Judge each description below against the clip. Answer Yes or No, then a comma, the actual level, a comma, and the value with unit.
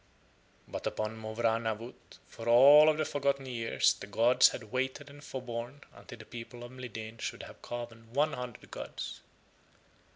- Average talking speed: Yes, average, 160 wpm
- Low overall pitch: Yes, low, 120 Hz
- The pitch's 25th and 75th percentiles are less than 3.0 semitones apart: Yes, narrow, 2.6 semitones